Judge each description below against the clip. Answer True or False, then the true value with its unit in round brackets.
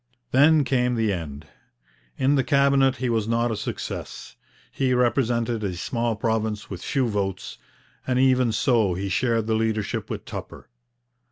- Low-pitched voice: True (115 Hz)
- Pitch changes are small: False (3.3 semitones)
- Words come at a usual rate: True (155 wpm)